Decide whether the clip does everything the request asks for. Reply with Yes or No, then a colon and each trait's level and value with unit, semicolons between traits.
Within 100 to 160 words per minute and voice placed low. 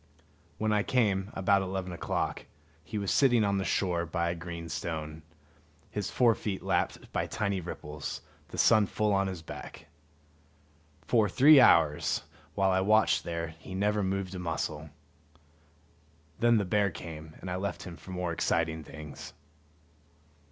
Yes: average, 155 wpm; very low, 95 Hz